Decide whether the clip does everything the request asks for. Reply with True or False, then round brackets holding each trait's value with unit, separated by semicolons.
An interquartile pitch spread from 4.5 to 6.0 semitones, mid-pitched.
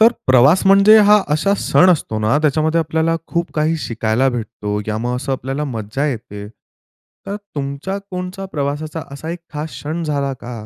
True (5.1 semitones; 150 Hz)